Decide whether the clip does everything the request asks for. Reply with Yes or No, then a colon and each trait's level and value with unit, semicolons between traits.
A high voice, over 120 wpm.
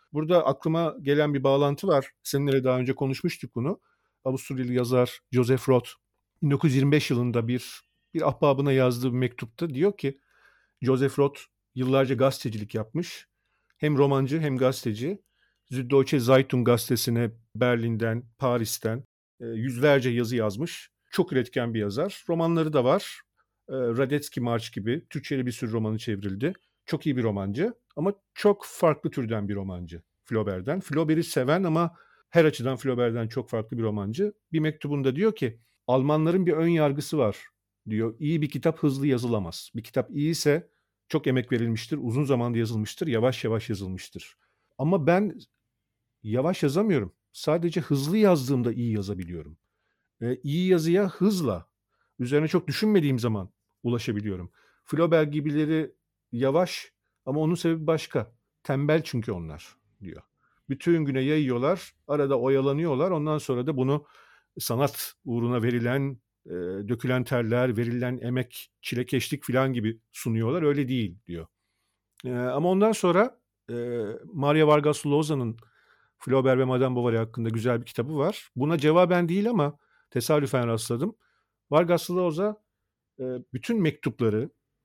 No: low, 135 Hz; average, 130 wpm